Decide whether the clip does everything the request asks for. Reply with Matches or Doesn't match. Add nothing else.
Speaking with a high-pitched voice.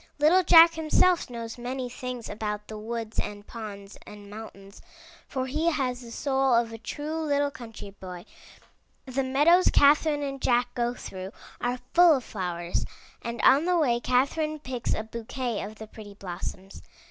Matches